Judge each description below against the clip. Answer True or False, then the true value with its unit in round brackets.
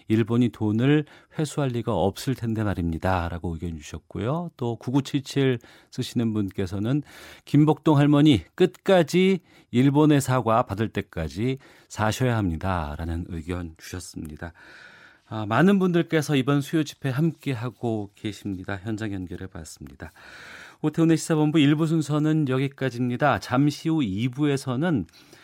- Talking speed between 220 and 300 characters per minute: True (290 characters per minute)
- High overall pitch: False (125 Hz)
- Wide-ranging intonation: True (7.2 semitones)